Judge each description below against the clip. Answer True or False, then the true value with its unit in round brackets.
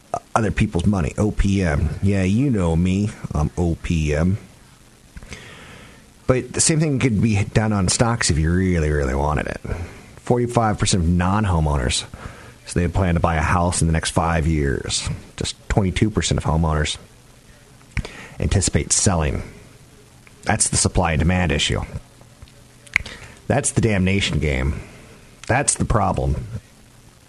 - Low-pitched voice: True (95 Hz)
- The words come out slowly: True (130 wpm)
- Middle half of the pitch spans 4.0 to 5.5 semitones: True (5.1 semitones)